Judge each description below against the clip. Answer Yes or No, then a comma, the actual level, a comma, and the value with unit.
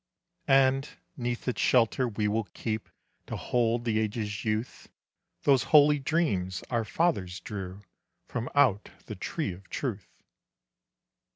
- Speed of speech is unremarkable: No, slow, 125 wpm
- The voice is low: Yes, low, 115 Hz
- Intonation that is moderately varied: Yes, average, 4.2 semitones